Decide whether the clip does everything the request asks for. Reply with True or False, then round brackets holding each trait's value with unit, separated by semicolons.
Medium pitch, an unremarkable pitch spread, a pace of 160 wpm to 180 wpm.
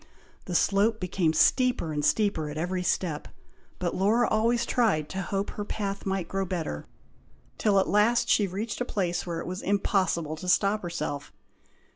False (195 Hz; 3.5 semitones; 170 wpm)